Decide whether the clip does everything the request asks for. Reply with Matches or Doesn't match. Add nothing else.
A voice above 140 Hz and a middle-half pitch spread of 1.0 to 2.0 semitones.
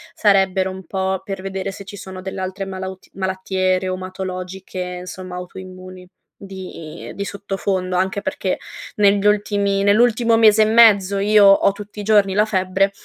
Matches